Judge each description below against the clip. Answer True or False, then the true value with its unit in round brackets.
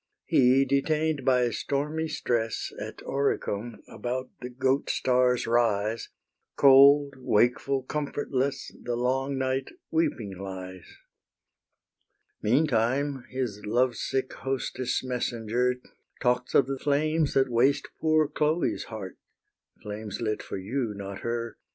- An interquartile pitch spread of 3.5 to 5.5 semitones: False (3.1 semitones)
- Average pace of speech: False (110 wpm)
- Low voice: True (125 Hz)